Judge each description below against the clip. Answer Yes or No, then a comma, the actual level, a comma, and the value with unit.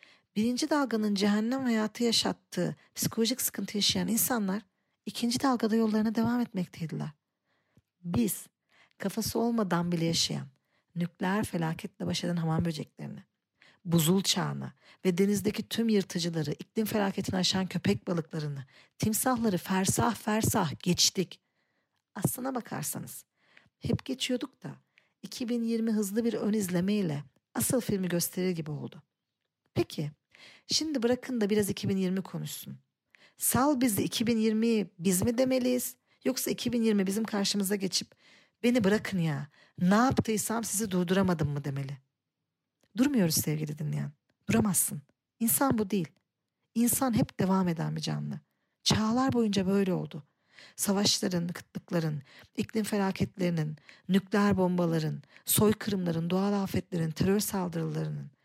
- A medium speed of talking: Yes, average, 115 wpm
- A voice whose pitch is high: Yes, high, 195 Hz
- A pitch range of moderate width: Yes, average, 4.8 semitones